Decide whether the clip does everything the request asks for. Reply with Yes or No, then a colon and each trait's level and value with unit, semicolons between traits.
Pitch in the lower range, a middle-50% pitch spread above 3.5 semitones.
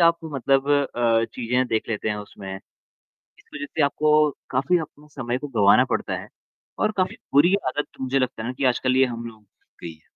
Yes: low, 130 Hz; average, 4.3 semitones